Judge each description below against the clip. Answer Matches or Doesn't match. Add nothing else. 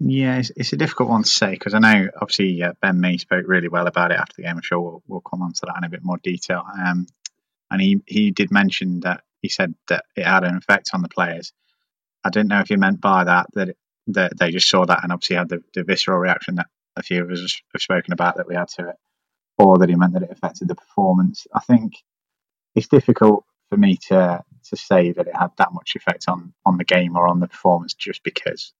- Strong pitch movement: Matches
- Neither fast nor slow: Doesn't match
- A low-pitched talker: Matches